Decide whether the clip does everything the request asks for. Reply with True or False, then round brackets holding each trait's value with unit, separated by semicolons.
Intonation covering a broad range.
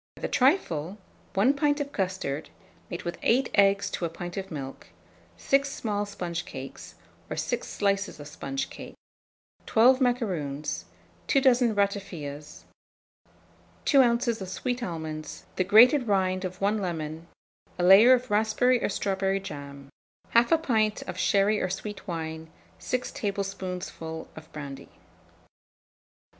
True (5.9 semitones)